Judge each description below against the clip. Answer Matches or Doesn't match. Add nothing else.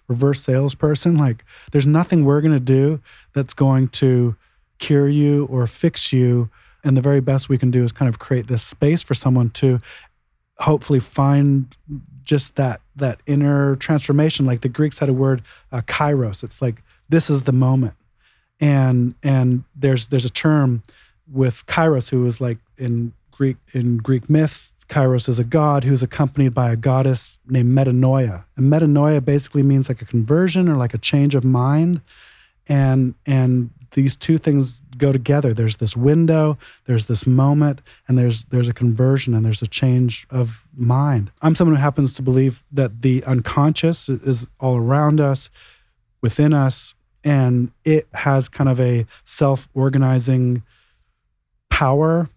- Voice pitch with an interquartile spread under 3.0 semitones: Matches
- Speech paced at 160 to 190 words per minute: Matches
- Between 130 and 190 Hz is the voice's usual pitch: Matches